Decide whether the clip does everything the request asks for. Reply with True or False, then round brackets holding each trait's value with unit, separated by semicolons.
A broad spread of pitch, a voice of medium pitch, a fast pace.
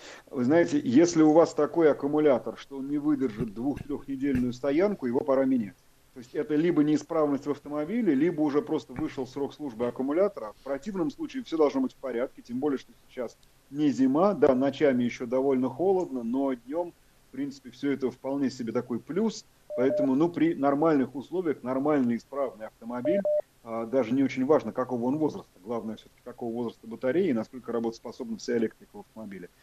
True (6.8 semitones; 145 Hz; 175 wpm)